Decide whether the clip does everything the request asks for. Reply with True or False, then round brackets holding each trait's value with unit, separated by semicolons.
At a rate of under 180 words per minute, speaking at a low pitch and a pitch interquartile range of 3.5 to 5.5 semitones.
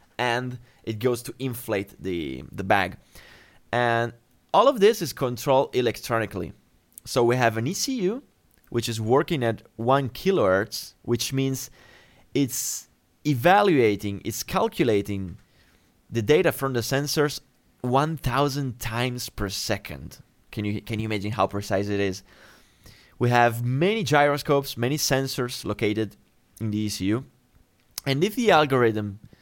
True (140 wpm; 120 Hz; 4.0 semitones)